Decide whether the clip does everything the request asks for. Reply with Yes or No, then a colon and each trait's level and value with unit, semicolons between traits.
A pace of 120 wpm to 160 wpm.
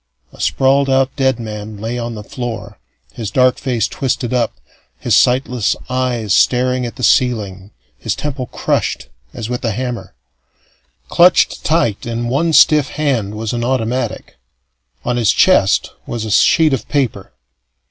Yes: average, 150 wpm